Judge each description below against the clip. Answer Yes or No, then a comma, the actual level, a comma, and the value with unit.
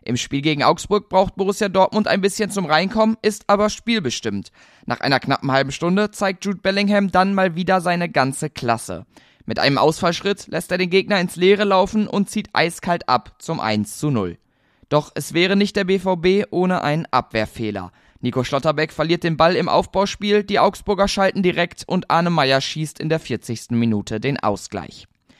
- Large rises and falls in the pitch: Yes, wide, 6.5 semitones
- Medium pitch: Yes, medium, 175 Hz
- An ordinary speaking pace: Yes, average, 180 wpm